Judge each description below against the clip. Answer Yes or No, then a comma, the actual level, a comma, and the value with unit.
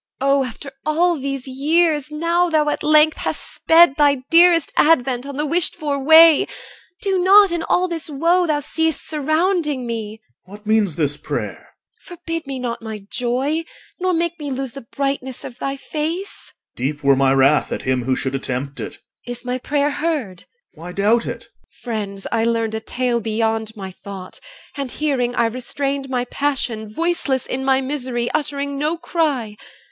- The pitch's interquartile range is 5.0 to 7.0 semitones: Yes, wide, 5.5 semitones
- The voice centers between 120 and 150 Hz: No, very high, 275 Hz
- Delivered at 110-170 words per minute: No, average, 185 wpm